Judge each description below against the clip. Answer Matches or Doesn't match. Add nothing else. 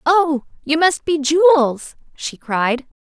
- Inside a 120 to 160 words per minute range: Matches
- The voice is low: Doesn't match